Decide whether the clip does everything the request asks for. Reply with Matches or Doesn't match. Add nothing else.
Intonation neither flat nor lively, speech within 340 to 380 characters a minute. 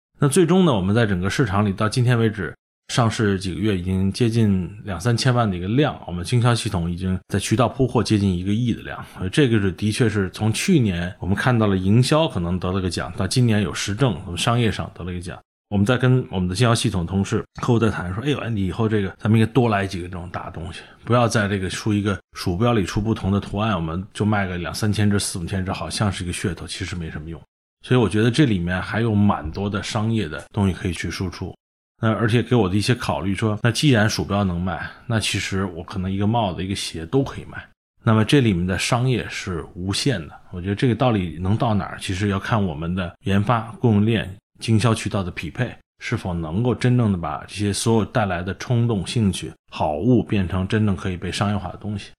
Matches